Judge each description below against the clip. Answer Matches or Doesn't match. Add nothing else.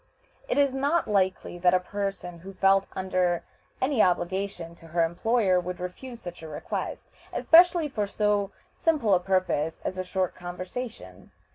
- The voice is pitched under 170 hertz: Doesn't match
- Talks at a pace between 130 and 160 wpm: Matches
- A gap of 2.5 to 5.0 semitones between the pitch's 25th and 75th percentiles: Matches